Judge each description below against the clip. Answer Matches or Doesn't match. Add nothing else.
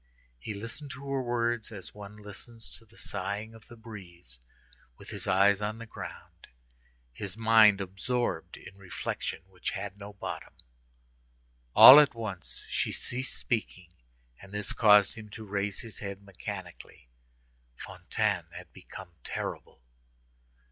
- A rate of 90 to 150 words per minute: Matches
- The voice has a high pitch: Doesn't match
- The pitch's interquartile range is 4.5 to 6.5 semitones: Doesn't match